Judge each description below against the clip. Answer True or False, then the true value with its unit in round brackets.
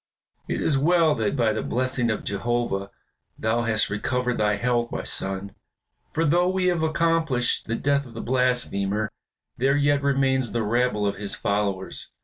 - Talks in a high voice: False (120 Hz)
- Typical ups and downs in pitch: True (4.6 semitones)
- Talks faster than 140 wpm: True (165 wpm)